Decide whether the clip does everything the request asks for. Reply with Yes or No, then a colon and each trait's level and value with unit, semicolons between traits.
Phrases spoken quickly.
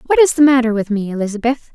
Yes: fast, 240 wpm